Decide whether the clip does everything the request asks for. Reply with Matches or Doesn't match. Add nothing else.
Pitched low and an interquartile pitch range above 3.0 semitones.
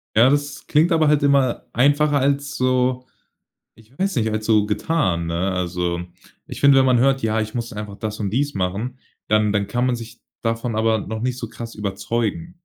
Matches